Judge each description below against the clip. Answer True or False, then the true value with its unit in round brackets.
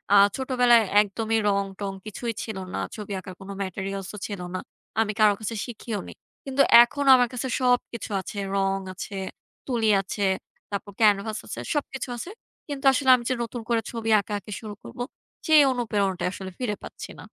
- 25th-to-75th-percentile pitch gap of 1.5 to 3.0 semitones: False (3.5 semitones)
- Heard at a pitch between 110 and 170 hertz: False (220 Hz)